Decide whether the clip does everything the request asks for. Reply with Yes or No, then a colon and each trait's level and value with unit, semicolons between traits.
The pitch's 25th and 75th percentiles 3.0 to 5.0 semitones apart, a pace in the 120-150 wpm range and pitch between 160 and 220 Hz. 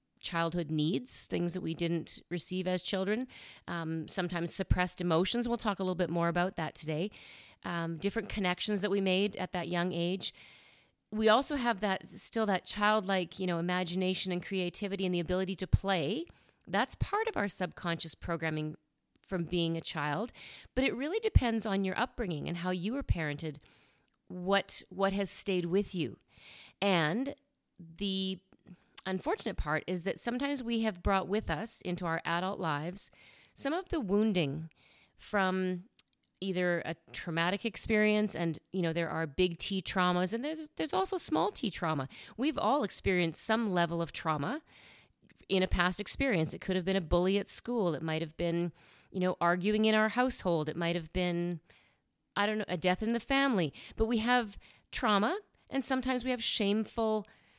No: average, 3.8 semitones; average, 175 wpm; medium, 185 Hz